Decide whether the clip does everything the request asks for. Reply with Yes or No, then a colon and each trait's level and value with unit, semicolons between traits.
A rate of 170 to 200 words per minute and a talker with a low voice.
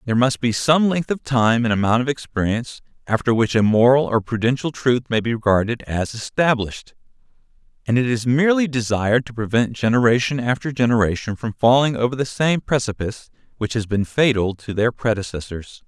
Yes: average, 175 wpm; low, 120 Hz